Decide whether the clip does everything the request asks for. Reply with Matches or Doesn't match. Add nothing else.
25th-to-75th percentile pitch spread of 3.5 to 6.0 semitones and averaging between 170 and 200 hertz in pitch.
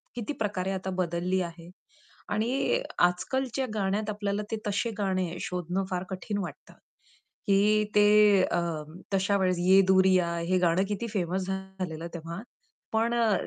Doesn't match